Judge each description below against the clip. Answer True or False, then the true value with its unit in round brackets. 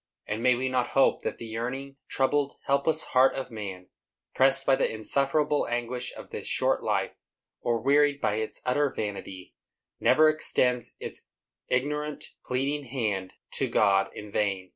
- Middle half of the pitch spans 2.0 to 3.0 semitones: False (4.2 semitones)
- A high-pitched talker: False (125 Hz)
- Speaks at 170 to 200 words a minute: False (155 wpm)